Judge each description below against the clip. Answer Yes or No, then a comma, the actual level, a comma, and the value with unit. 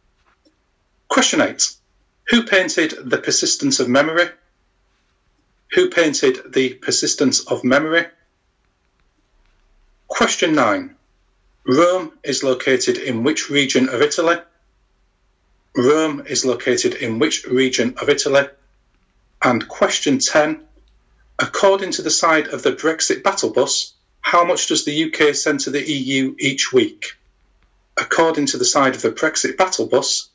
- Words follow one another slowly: Yes, slow, 125 wpm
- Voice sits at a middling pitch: Yes, medium, 165 Hz